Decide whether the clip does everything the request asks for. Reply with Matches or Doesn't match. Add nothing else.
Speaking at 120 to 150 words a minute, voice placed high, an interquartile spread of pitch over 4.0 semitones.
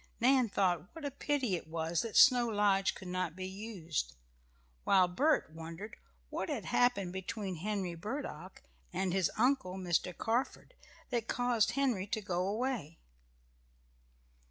Matches